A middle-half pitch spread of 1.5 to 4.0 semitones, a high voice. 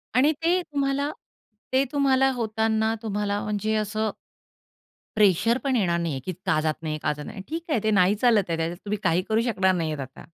No: average, 5.2 semitones; high, 210 Hz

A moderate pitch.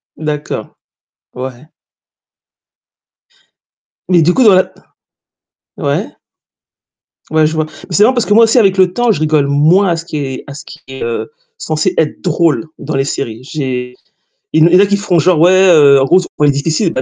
Yes: medium, 155 Hz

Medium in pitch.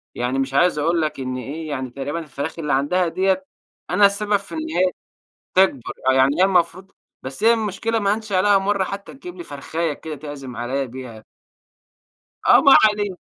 Yes: medium, 170 Hz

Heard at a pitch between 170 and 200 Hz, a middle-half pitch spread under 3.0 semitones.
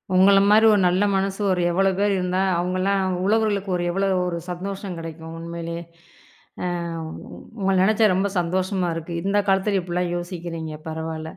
Yes: medium, 185 Hz; narrow, 2.6 semitones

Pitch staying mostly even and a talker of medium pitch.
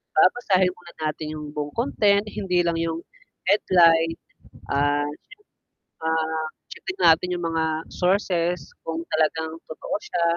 Yes: narrow, 2.2 semitones; medium, 165 Hz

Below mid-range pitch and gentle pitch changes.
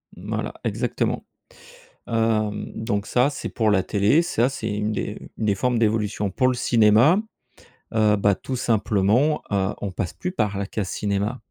No: low, 110 Hz; average, 3.0 semitones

